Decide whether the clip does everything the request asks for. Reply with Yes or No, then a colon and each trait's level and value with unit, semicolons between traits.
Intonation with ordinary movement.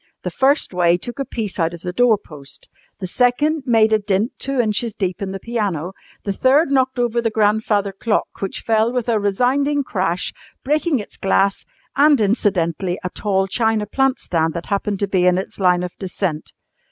Yes: average, 4.6 semitones